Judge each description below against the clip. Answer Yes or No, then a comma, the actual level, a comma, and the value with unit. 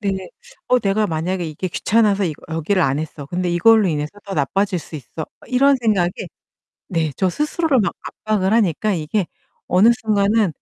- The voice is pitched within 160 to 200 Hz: Yes, high, 190 Hz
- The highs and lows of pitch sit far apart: No, average, 4.6 semitones